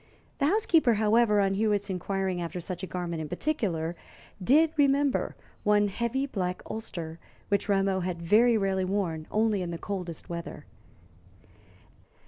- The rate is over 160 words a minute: No, average, 140 wpm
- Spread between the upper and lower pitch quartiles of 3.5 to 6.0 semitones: Yes, average, 4.0 semitones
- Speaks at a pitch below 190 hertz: No, high, 195 Hz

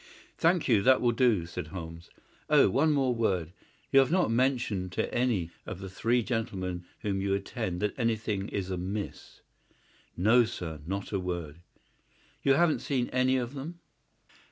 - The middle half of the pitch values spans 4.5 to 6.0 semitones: Yes, wide, 5.6 semitones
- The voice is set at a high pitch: No, low, 110 Hz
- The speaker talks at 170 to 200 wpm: No, average, 160 wpm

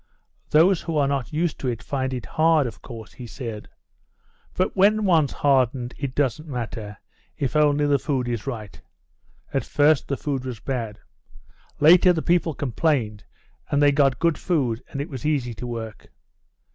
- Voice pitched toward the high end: No, medium, 140 Hz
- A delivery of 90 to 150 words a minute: No, average, 170 wpm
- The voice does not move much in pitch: No, average, 4.2 semitones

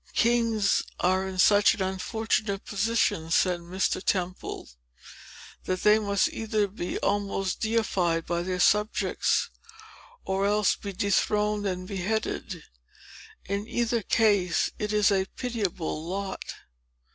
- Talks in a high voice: Yes, high, 200 Hz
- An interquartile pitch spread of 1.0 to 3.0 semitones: Yes, narrow, 2.4 semitones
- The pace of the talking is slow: Yes, slow, 120 wpm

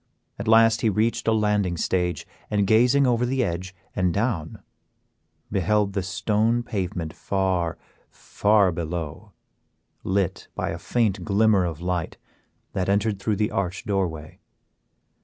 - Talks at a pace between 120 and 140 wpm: Yes, slow, 135 wpm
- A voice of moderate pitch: No, low, 100 Hz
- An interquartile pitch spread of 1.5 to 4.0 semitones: Yes, average, 3.6 semitones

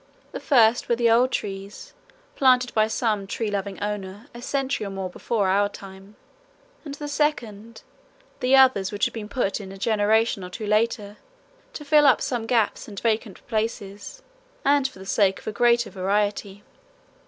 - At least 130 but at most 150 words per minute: No, average, 175 wpm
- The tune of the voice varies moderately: Yes, average, 3.3 semitones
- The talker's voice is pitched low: No, high, 215 Hz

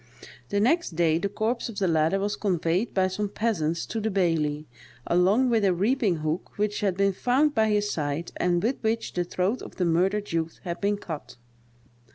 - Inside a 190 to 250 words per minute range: Yes, average, 200 wpm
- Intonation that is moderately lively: Yes, average, 4.1 semitones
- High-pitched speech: Yes, high, 195 Hz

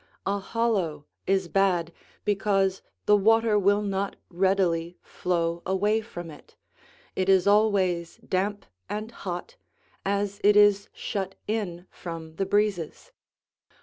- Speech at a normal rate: No, slow, 120 wpm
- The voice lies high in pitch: Yes, high, 195 Hz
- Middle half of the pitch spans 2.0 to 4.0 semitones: Yes, average, 2.7 semitones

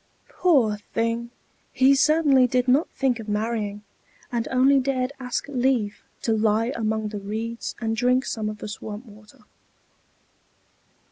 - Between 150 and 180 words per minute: No, average, 140 wpm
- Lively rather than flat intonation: No, average, 3.2 semitones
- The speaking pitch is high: Yes, high, 235 Hz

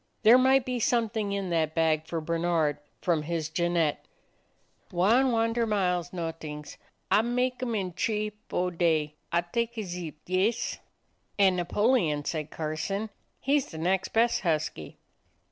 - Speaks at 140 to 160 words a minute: Yes, average, 145 wpm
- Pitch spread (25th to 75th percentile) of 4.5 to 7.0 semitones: Yes, wide, 5.6 semitones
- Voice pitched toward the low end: No, medium, 180 Hz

